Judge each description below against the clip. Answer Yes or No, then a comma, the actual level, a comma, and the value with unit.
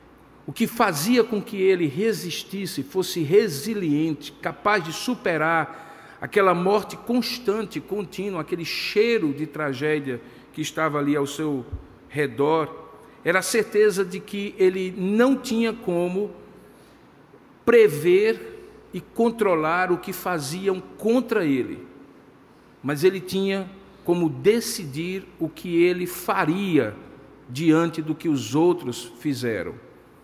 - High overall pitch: No, medium, 180 Hz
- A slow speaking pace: Yes, slow, 115 wpm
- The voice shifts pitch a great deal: No, average, 4.9 semitones